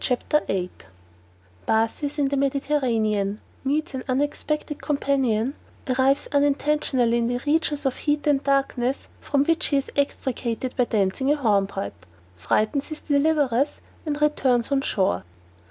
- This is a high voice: Yes, very high, 275 Hz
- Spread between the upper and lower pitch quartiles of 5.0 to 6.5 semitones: No, average, 3.7 semitones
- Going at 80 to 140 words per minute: Yes, slow, 135 wpm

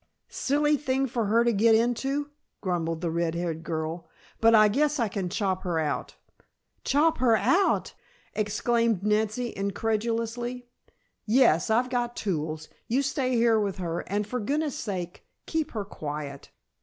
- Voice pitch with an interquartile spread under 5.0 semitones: No, wide, 5.5 semitones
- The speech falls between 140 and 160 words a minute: Yes, average, 150 wpm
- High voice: Yes, high, 220 Hz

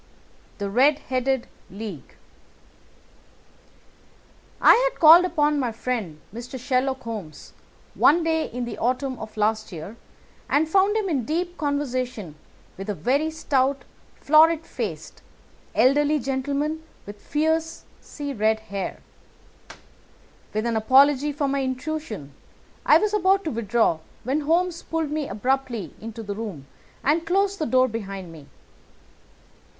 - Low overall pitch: No, very high, 265 Hz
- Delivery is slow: Yes, slow, 130 wpm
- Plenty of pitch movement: Yes, wide, 5.9 semitones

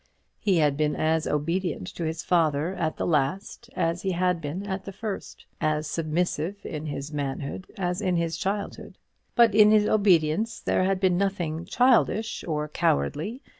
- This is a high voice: No, medium, 175 Hz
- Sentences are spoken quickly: No, average, 170 wpm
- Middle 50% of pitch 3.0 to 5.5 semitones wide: Yes, average, 4.2 semitones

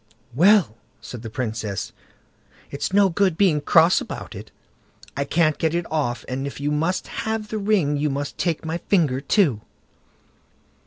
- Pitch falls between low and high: Yes, medium, 155 Hz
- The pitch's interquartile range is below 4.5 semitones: No, average, 5.3 semitones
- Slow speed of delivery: No, average, 160 wpm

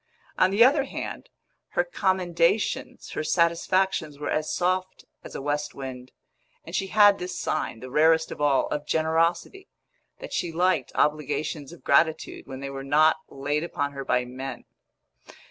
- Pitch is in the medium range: Yes, medium, 160 Hz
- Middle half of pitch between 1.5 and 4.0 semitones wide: No, average, 4.5 semitones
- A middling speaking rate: Yes, average, 160 wpm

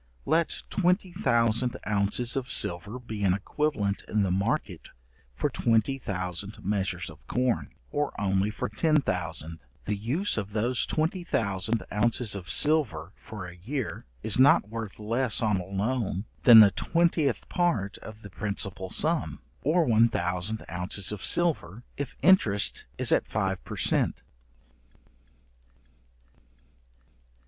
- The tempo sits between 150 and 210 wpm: No, average, 140 wpm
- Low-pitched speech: Yes, low, 110 Hz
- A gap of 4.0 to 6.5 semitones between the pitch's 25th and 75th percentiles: Yes, average, 5.0 semitones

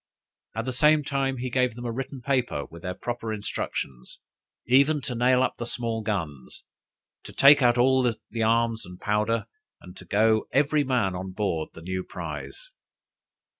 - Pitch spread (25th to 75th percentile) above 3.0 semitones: Yes, average, 4.2 semitones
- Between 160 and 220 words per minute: Yes, average, 170 wpm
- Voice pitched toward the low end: Yes, low, 115 Hz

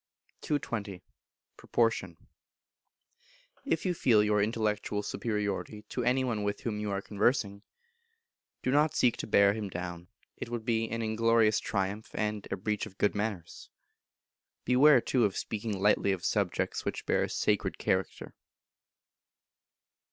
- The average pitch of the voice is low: Yes, low, 105 Hz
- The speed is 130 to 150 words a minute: Yes, average, 140 wpm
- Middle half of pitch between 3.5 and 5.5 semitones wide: No, narrow, 2.4 semitones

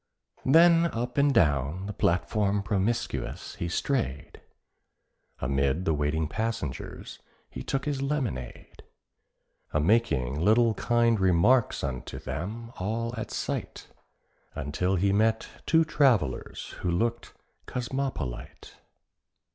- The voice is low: Yes, low, 105 Hz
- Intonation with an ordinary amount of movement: No, wide, 7.2 semitones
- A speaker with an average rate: No, slow, 105 wpm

